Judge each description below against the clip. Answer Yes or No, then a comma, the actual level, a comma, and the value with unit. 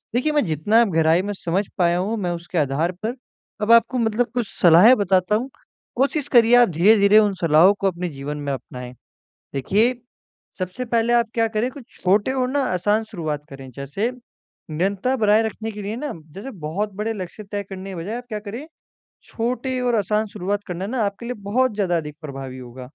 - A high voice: Yes, high, 205 Hz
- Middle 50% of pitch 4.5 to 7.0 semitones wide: Yes, average, 5.1 semitones